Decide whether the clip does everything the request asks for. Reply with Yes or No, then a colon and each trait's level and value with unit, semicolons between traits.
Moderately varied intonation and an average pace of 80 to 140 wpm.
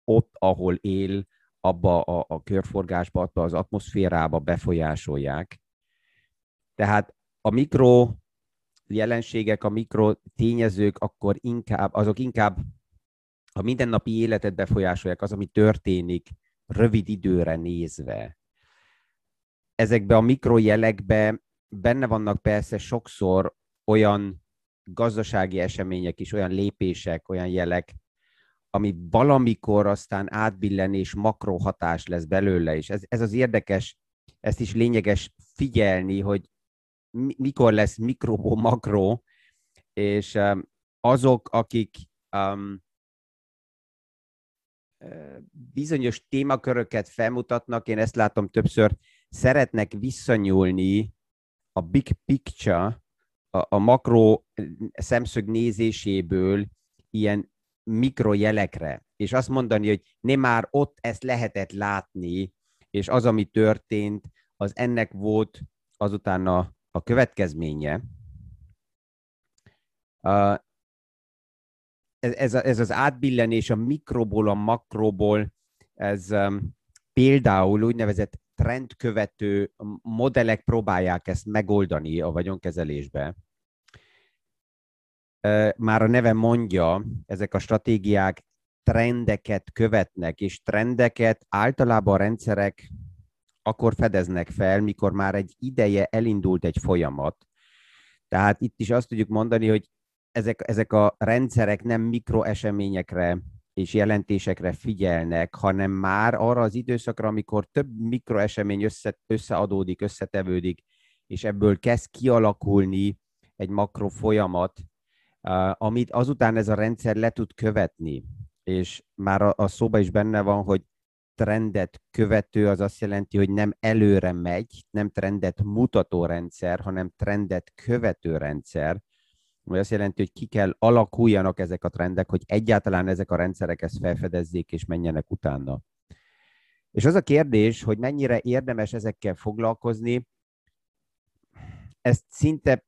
Yes: average, 3.4 semitones; average, 110 wpm